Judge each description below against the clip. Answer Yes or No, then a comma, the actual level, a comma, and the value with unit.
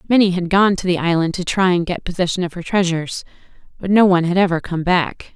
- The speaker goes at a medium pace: No, fast, 235 wpm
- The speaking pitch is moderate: Yes, medium, 180 Hz